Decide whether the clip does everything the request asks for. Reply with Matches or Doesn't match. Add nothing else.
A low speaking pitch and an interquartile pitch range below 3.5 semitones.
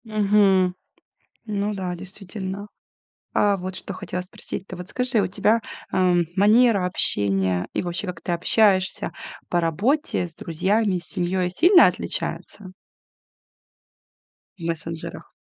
Doesn't match